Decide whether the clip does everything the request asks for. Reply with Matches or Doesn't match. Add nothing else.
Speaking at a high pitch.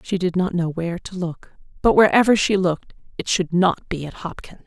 Doesn't match